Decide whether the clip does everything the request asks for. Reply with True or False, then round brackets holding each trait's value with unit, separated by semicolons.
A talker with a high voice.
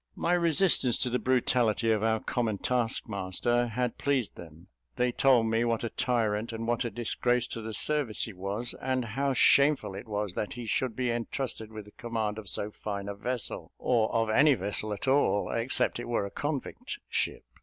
False (115 Hz)